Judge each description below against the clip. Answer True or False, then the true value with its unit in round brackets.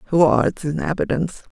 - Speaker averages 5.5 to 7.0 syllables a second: True (6.6 syllables/s)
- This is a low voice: False (155 Hz)